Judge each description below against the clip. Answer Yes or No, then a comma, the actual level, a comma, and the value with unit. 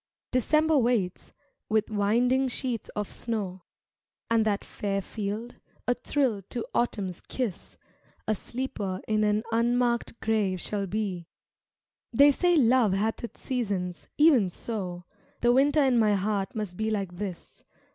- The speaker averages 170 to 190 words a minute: No, slow, 135 wpm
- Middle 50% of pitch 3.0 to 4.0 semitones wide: Yes, average, 3.7 semitones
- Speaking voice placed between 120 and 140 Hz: No, high, 220 Hz